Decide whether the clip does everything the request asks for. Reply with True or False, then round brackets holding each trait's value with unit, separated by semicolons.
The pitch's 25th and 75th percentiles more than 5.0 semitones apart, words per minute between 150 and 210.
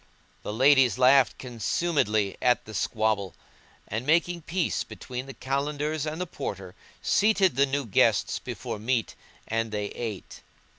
False (5.5 semitones; 140 wpm)